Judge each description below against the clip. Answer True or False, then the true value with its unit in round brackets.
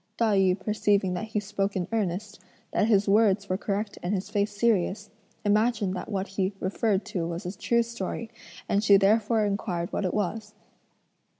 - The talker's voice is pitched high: True (205 Hz)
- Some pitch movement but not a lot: False (2.2 semitones)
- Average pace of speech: True (180 wpm)